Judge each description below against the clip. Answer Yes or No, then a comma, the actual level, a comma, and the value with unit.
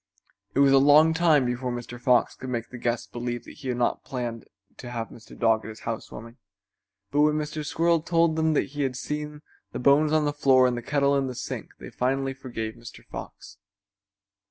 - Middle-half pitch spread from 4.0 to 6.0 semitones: No, average, 3.6 semitones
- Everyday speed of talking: No, fast, 210 wpm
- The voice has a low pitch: Yes, low, 130 Hz